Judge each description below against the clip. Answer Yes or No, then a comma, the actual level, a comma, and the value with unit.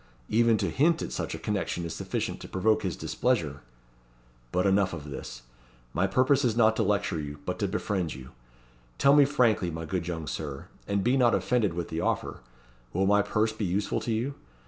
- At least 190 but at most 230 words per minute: Yes, average, 200 wpm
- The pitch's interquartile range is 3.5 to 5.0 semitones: No, wide, 5.5 semitones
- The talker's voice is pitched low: Yes, low, 100 Hz